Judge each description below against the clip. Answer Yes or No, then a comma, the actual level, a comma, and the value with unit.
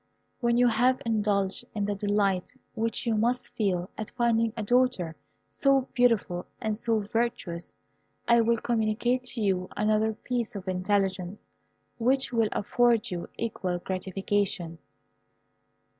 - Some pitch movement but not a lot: Yes, average, 3.4 semitones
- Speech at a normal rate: No, slow, 130 wpm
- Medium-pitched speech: No, high, 215 Hz